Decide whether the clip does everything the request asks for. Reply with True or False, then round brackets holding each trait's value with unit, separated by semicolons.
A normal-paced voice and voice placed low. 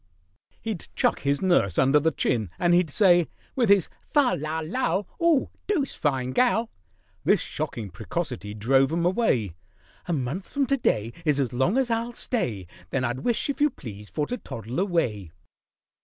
False (170 wpm; 160 Hz)